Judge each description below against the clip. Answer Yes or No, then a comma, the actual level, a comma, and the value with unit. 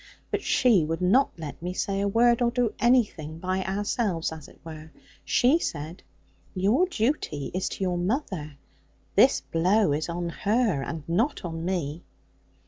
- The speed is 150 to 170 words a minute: Yes, average, 160 wpm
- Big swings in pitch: Yes, wide, 5.7 semitones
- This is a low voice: No, medium, 185 Hz